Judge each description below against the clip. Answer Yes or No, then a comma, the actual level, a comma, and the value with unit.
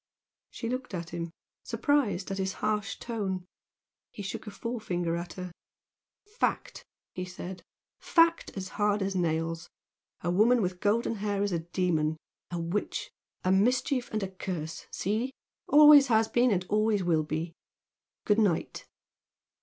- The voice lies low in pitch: No, high, 195 Hz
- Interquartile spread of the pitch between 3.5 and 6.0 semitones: Yes, average, 4.0 semitones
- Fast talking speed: No, average, 145 wpm